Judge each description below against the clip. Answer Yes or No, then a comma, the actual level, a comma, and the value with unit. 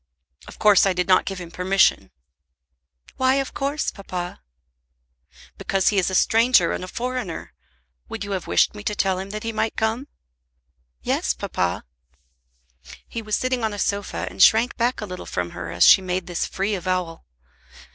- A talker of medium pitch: No, high, 195 Hz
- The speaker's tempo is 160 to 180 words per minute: Yes, average, 175 wpm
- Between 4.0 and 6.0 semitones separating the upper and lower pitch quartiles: No, average, 3.6 semitones